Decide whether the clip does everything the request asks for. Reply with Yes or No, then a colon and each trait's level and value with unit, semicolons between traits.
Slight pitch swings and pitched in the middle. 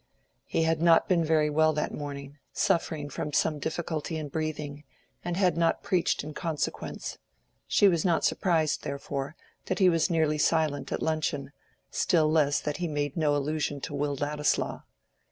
Yes: narrow, 2.1 semitones; medium, 155 Hz